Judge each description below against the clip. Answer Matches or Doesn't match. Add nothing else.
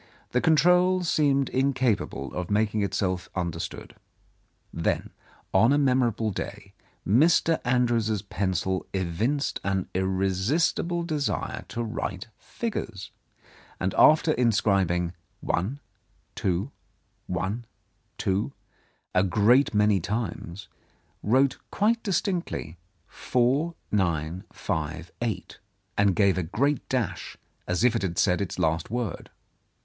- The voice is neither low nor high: Doesn't match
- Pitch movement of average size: Doesn't match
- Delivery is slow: Matches